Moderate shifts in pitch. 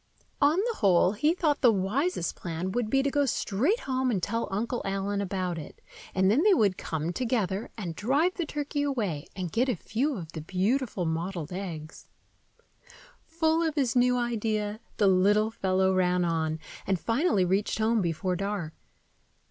No: wide, 6.1 semitones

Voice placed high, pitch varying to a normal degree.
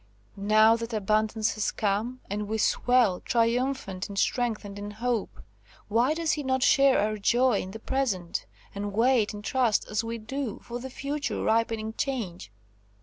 Yes: high, 225 Hz; average, 3.4 semitones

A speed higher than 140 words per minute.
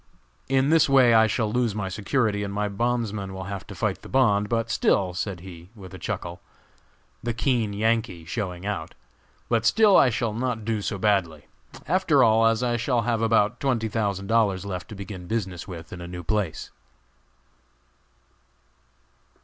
Yes: average, 175 wpm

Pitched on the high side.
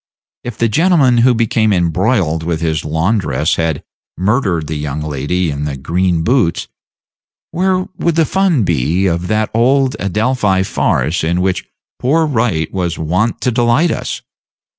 No: very low, 95 Hz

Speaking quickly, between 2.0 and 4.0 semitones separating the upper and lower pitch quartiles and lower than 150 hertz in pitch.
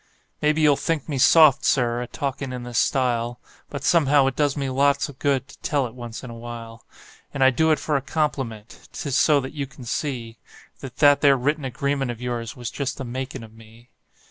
Yes: fast, 220 wpm; average, 2.9 semitones; low, 135 Hz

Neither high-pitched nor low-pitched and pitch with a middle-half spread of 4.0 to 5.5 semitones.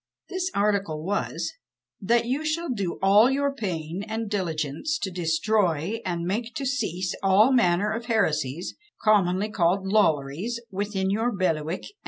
No: high, 200 Hz; average, 4.7 semitones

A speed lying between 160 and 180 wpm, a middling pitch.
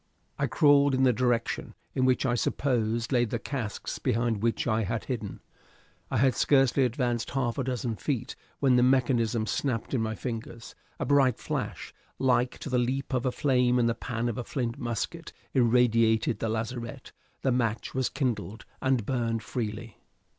No: average, 175 wpm; low, 120 Hz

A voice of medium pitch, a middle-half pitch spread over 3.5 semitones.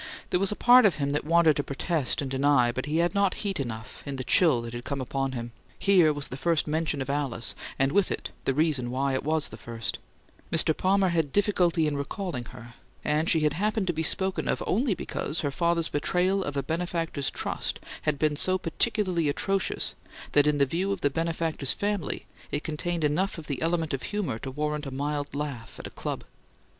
Yes: medium, 155 Hz; average, 4.1 semitones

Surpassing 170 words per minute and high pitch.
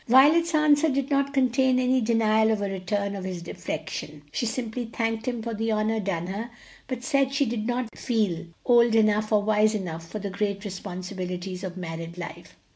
Yes: average, 190 wpm; high, 220 Hz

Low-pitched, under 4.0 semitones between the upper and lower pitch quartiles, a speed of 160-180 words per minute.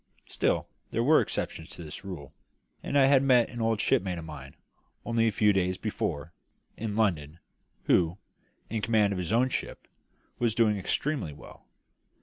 No: low, 105 Hz; wide, 5.4 semitones; average, 165 wpm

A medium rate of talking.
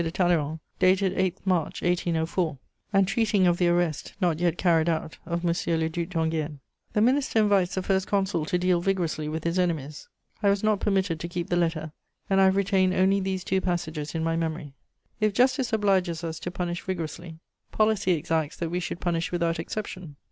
Yes: average, 195 wpm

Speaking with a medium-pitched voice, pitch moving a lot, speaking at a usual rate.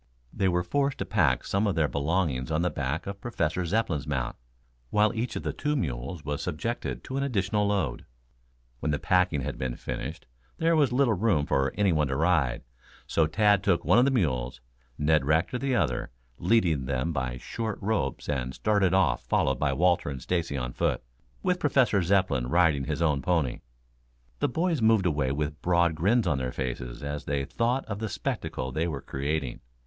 No: very low, 85 Hz; wide, 7.1 semitones; average, 190 wpm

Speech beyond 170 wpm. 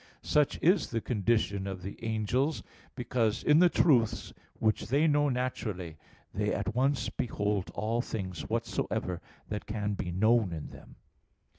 No: average, 145 wpm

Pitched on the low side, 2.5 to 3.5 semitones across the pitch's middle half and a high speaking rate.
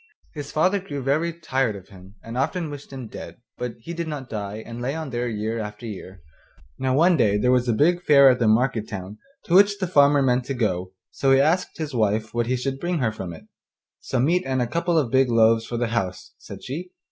No: low, 125 Hz; average, 5.1 semitones; fast, 240 wpm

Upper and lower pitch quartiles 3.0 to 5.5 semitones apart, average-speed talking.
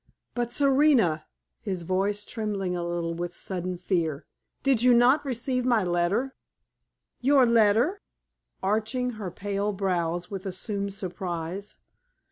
No: average, 5.2 semitones; slow, 120 wpm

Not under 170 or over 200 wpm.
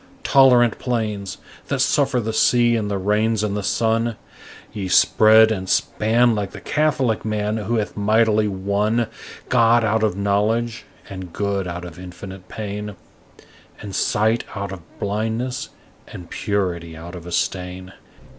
No: average, 145 wpm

